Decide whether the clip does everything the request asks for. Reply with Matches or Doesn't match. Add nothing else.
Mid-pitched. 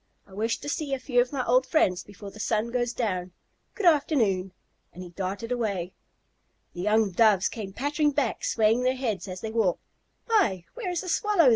Doesn't match